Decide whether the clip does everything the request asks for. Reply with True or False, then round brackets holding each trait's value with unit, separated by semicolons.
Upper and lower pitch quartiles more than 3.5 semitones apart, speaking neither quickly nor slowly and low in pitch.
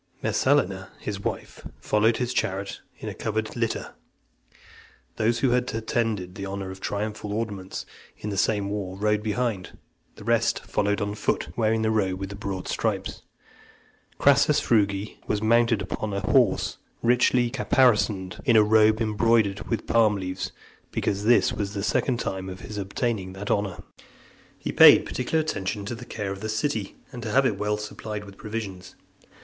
False (2.4 semitones; 170 wpm; 105 Hz)